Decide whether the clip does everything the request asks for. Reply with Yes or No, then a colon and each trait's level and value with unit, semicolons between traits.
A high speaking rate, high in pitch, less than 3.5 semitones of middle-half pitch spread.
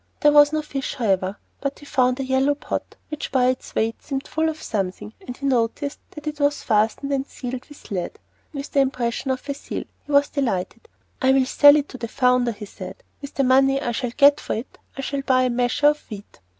Yes: fast, 230 wpm; very high, 265 Hz; average, 2.9 semitones